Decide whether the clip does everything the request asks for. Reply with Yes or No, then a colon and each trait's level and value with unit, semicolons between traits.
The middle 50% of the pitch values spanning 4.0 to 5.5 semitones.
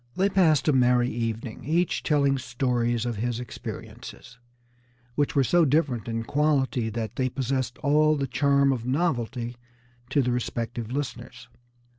No: average, 3.2 semitones